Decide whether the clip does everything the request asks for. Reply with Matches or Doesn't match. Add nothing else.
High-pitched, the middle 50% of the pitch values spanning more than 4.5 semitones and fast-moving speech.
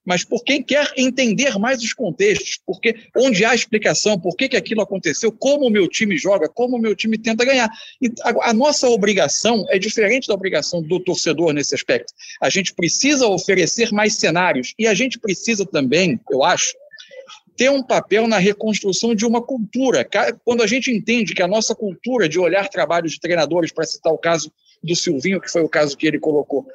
Matches